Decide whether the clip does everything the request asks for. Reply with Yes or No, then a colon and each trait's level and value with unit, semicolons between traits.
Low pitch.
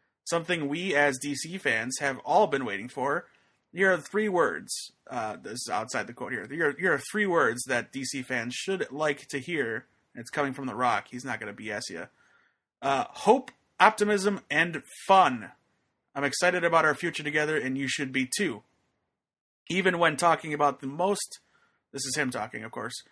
No: medium, 150 Hz